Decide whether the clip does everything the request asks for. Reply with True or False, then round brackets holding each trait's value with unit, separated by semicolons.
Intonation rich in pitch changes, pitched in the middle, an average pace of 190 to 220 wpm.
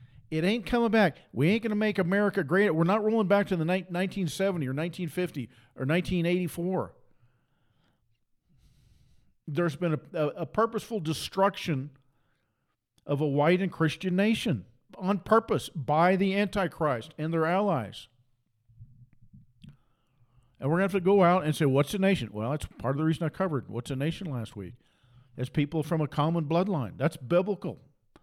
False (6.4 semitones; 160 Hz; 165 wpm)